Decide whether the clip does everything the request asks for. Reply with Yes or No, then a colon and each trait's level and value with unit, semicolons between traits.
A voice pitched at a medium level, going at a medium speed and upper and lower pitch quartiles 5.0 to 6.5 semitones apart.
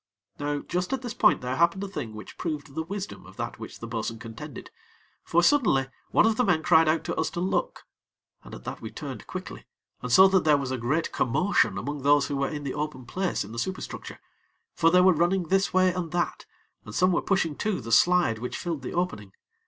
No: medium, 165 Hz; fast, 230 wpm; wide, 5.4 semitones